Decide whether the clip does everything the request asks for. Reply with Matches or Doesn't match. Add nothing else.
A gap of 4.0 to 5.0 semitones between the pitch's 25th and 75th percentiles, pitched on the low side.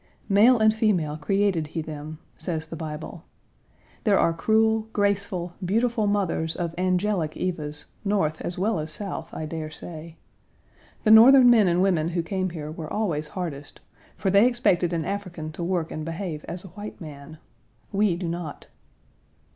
Doesn't match